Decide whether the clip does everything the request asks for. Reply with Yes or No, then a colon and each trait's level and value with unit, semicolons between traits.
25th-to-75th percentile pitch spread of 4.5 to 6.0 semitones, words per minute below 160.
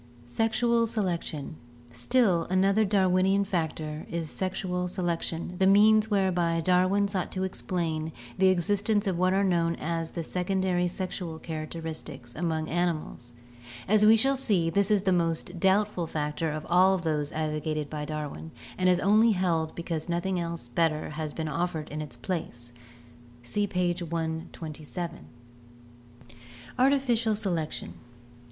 No: average, 3.3 semitones; average, 140 wpm